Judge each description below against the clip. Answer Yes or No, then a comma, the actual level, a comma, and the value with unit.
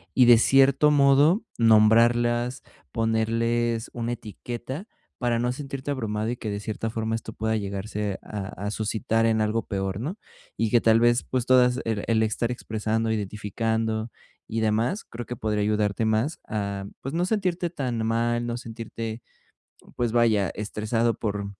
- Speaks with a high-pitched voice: No, low, 115 Hz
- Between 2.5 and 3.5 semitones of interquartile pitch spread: No, narrow, 2.0 semitones